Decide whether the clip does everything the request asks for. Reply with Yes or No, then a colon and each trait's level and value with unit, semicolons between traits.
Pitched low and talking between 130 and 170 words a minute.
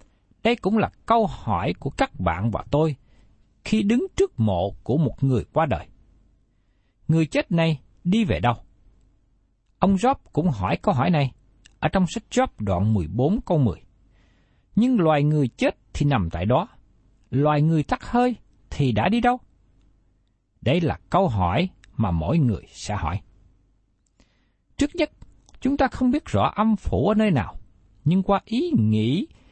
Yes: low, 125 Hz; slow, 165 wpm